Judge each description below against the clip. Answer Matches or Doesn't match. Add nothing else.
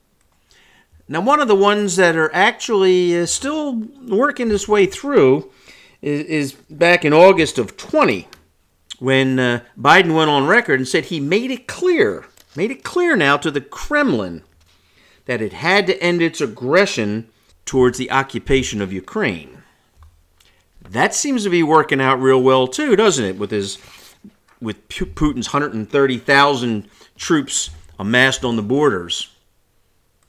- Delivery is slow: Doesn't match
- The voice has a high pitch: Doesn't match